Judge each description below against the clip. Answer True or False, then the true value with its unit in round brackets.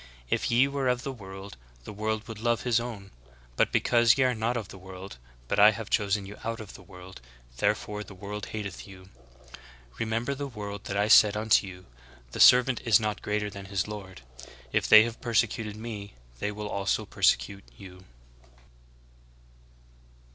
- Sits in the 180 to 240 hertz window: False (105 Hz)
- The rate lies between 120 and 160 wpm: False (180 wpm)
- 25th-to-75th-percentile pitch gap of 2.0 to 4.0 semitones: True (2.7 semitones)